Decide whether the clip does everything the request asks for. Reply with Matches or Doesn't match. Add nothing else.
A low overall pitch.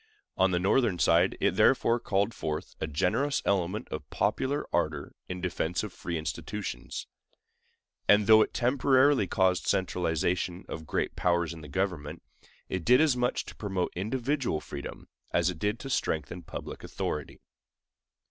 Matches